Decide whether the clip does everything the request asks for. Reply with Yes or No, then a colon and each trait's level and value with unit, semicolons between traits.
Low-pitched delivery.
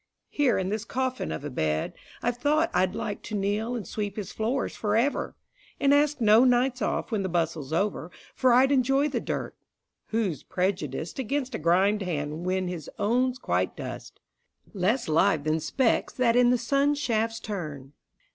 No: high, 215 Hz